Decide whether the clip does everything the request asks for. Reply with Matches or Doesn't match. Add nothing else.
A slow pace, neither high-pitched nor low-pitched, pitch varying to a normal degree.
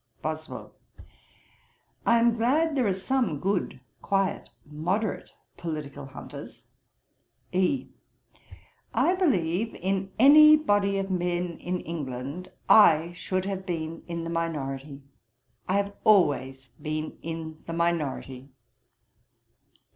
Matches